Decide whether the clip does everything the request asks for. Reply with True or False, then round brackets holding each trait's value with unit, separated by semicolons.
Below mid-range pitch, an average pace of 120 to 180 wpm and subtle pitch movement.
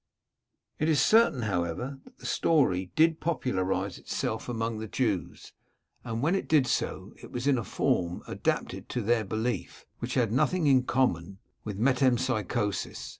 False (120 Hz; 155 wpm; 4.8 semitones)